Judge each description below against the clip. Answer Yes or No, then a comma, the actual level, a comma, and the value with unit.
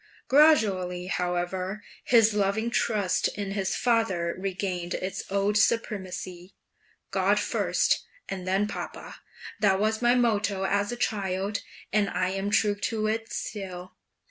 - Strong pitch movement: No, narrow, 2.5 semitones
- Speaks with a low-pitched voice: No, high, 200 Hz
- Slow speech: Yes, slow, 130 wpm